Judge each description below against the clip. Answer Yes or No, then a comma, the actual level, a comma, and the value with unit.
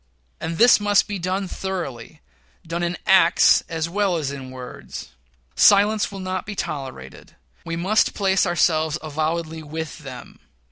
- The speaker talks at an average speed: Yes, average, 145 wpm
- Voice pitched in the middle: Yes, medium, 170 Hz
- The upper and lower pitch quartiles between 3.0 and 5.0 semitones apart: Yes, average, 3.7 semitones